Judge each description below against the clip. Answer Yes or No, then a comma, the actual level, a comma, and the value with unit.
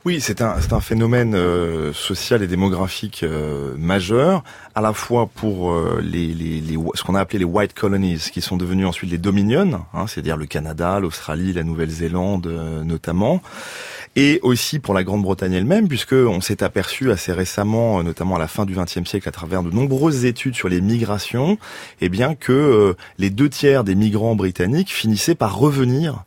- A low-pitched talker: Yes, low, 100 Hz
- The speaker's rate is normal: Yes, average, 190 wpm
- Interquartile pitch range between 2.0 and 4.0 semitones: No, average, 5.1 semitones